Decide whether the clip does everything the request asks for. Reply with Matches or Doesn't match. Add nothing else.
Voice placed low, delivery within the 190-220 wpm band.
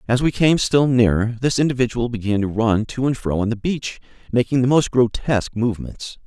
Matches